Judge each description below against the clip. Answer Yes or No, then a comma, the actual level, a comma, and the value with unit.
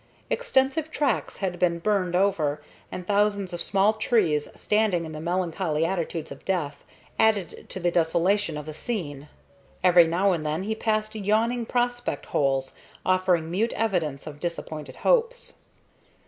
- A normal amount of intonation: Yes, average, 5.0 semitones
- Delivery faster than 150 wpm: No, average, 145 wpm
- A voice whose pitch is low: No, medium, 185 Hz